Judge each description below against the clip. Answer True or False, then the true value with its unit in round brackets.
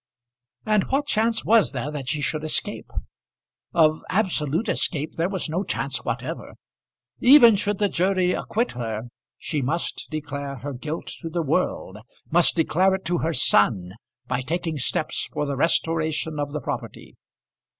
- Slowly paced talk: False (155 wpm)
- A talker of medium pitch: True (160 Hz)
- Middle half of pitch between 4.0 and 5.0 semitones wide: True (4.7 semitones)